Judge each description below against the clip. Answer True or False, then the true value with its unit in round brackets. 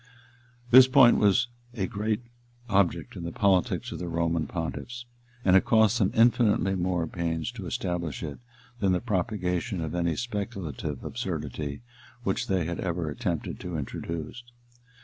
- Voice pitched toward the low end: True (95 Hz)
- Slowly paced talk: False (150 wpm)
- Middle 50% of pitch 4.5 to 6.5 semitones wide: True (4.8 semitones)